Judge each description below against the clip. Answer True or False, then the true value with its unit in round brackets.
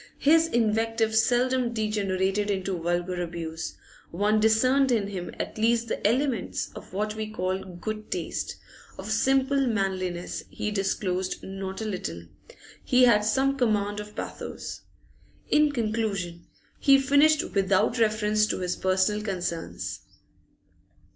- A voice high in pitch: True (210 Hz)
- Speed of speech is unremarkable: False (130 wpm)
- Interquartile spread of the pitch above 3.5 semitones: True (3.9 semitones)